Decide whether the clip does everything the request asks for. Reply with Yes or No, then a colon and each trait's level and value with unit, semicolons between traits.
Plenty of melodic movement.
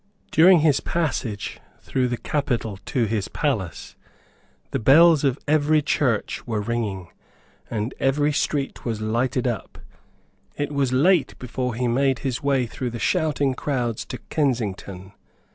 No: average, 4.1 semitones